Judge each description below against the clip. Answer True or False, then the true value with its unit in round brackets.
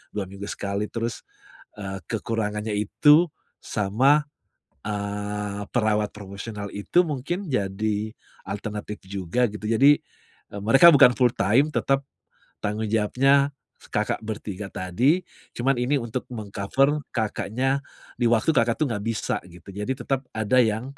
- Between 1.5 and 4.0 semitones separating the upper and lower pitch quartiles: False (4.4 semitones)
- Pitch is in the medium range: False (110 Hz)